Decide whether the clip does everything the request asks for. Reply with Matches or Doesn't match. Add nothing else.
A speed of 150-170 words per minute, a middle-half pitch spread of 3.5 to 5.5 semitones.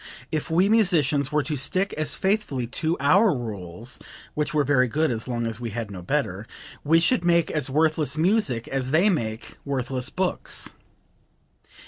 Matches